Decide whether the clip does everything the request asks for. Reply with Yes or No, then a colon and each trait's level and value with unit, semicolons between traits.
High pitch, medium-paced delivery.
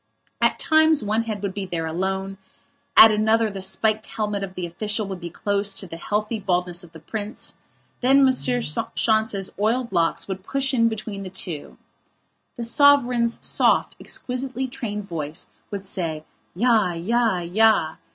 Yes: high, 210 Hz; average, 160 wpm